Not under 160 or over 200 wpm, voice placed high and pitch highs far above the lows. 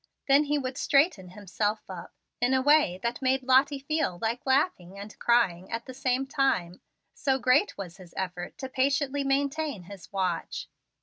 Yes: average, 170 wpm; very high, 255 Hz; wide, 6.2 semitones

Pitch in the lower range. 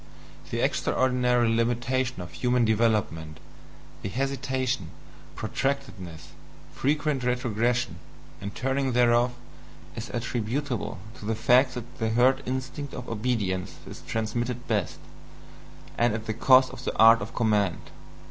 Yes: low, 120 Hz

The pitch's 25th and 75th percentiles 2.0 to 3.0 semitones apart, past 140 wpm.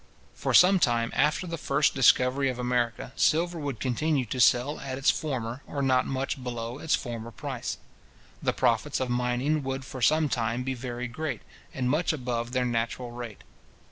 Yes: average, 2.7 semitones; average, 175 wpm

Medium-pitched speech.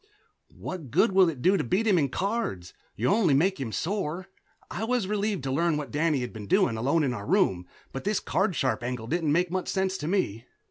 Yes: medium, 165 Hz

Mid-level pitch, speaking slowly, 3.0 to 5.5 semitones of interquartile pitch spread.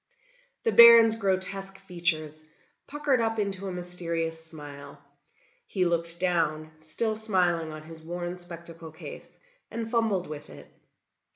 Yes: medium, 175 Hz; slow, 125 wpm; average, 3.6 semitones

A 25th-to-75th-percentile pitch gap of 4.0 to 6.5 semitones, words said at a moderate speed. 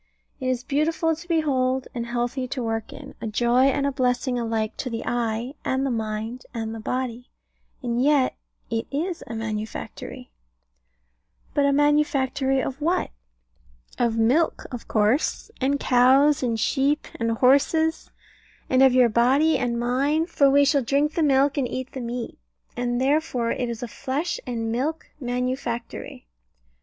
No: average, 3.1 semitones; average, 155 wpm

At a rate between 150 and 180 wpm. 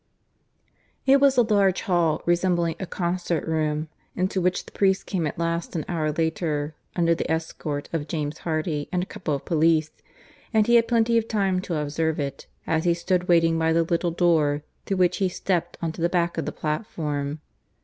No: average, 200 wpm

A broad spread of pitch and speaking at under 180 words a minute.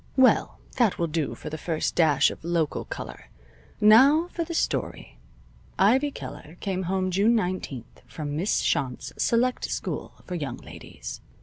Yes: wide, 6.9 semitones; average, 150 wpm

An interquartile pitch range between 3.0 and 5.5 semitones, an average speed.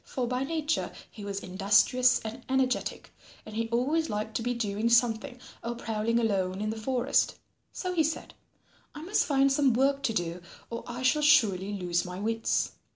Yes: average, 4.1 semitones; average, 180 wpm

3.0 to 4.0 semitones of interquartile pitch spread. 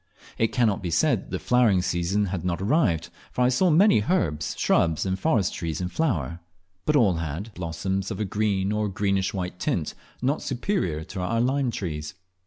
No: wide, 5.5 semitones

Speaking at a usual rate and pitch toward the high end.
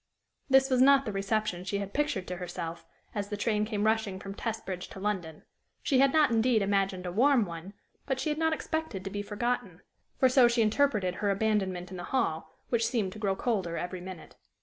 No: fast, 210 wpm; high, 210 Hz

